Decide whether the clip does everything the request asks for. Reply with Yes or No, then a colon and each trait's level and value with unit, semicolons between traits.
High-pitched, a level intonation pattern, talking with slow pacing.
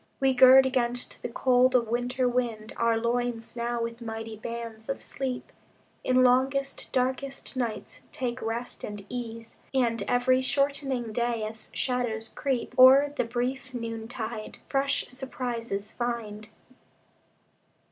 Yes: high, 245 Hz; narrow, 2.0 semitones; slow, 125 wpm